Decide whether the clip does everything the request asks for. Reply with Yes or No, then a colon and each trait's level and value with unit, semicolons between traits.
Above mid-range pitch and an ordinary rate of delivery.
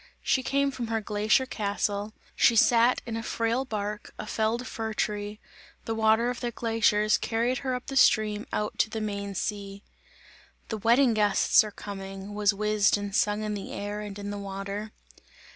Yes: high, 215 Hz; average, 180 wpm